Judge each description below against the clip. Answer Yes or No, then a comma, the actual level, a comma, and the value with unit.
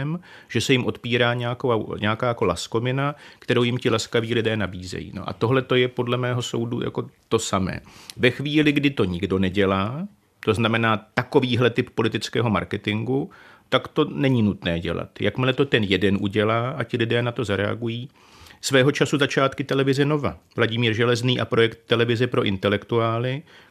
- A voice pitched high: No, low, 120 Hz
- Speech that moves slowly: No, average, 165 wpm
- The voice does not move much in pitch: No, average, 3.2 semitones